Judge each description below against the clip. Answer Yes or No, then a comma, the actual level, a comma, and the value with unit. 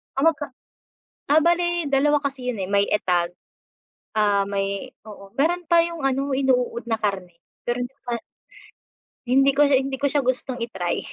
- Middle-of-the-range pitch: No, very high, 260 Hz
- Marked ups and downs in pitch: Yes, wide, 5.8 semitones